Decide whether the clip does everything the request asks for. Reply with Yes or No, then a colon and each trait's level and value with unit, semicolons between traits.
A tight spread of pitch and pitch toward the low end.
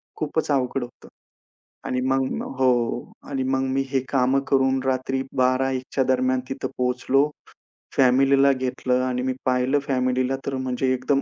Yes: narrow, 0.9 semitones; low, 130 Hz